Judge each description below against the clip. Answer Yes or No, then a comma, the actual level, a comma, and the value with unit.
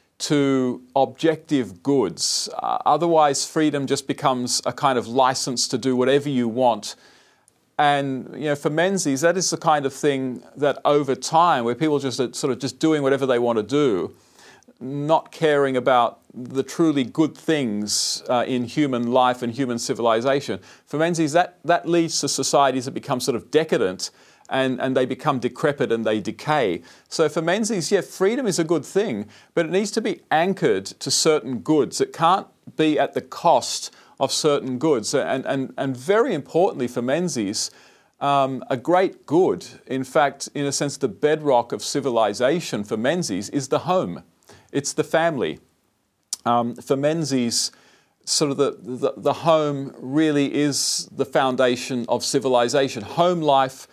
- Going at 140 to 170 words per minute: Yes, average, 165 wpm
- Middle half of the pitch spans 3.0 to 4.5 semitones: Yes, average, 3.5 semitones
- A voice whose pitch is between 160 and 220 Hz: No, medium, 140 Hz